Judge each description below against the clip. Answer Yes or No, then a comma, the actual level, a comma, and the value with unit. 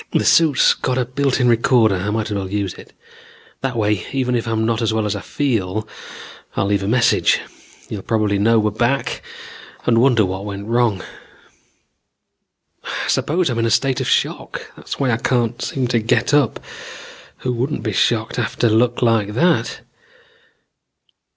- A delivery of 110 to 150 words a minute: No, average, 175 wpm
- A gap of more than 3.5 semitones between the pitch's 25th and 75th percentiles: No, average, 3.0 semitones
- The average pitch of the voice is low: Yes, low, 115 Hz